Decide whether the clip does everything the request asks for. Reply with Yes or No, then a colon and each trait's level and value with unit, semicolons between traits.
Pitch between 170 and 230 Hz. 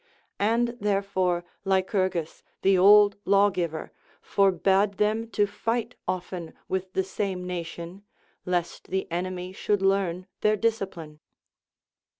Yes: high, 190 Hz